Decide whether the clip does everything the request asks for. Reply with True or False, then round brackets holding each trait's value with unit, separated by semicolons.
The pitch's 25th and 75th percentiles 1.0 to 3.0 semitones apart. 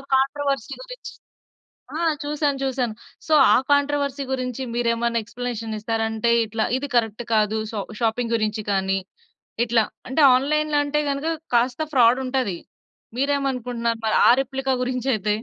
False (3.5 semitones)